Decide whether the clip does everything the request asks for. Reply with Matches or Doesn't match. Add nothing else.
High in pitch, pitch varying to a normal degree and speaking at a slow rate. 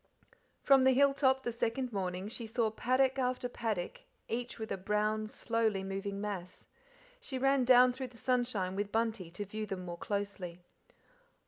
Doesn't match